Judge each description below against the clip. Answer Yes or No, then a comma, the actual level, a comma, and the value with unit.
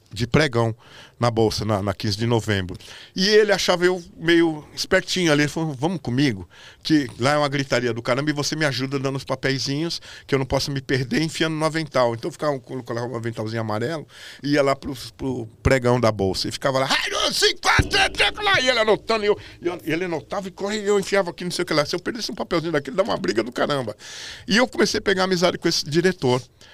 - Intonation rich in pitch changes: Yes, wide, 6.4 semitones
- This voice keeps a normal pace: No, fast, 240 wpm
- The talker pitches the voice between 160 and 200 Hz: No, medium, 145 Hz